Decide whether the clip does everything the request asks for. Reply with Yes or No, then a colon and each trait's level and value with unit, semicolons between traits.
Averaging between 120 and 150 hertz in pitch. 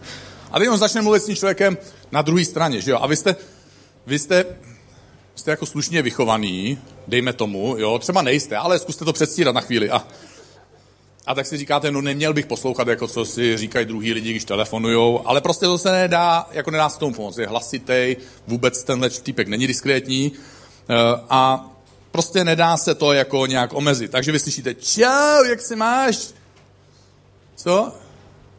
Yes: low, 135 Hz